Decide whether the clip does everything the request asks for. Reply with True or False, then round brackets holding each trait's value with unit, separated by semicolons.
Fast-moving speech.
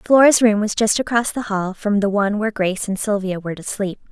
True (250 wpm)